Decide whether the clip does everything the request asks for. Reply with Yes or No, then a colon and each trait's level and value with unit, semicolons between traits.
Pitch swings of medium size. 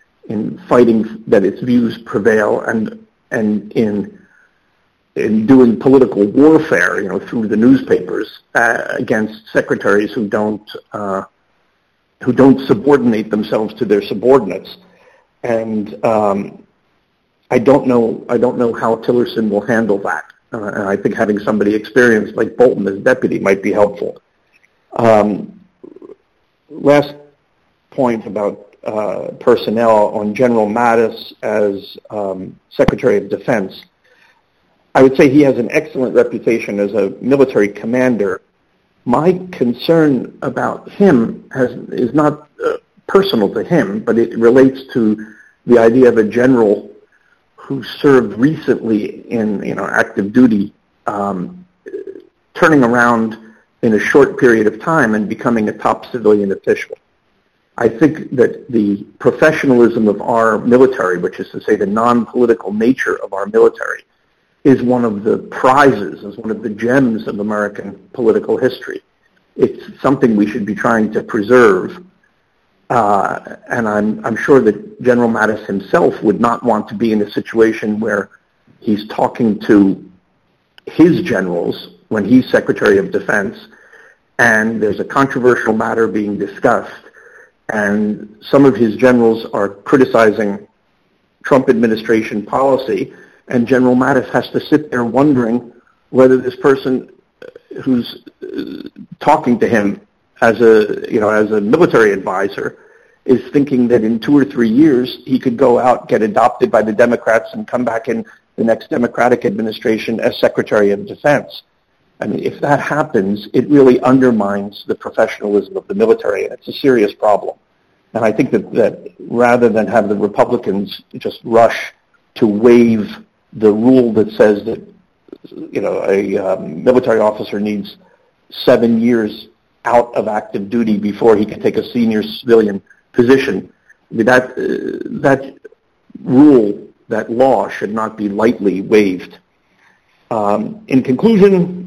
Yes: average, 4.4 semitones